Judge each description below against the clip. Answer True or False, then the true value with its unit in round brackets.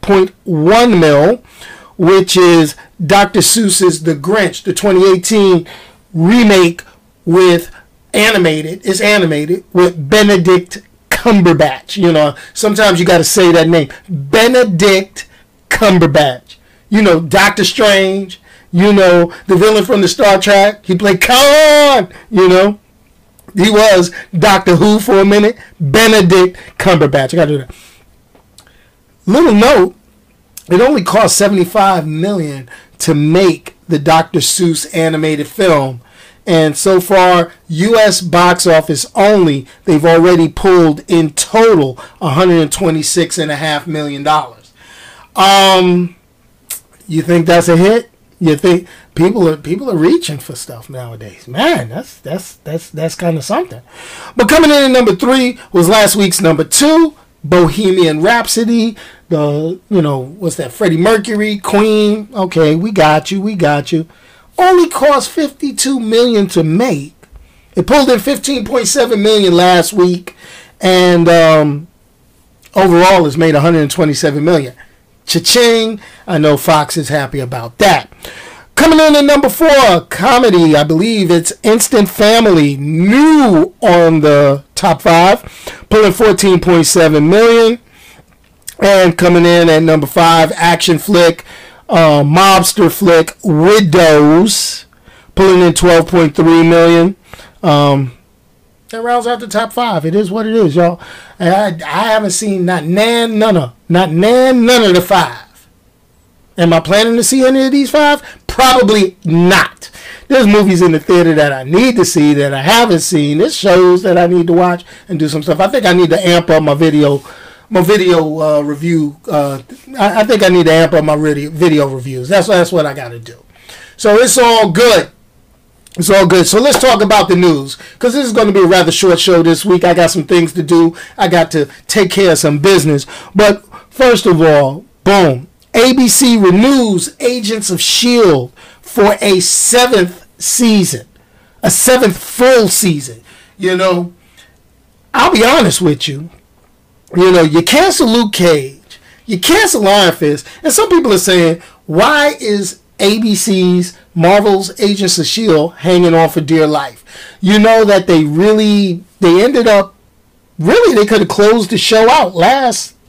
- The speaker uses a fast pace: False (150 wpm)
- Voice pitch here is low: False (180 Hz)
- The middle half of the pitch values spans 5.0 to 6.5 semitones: False (4.6 semitones)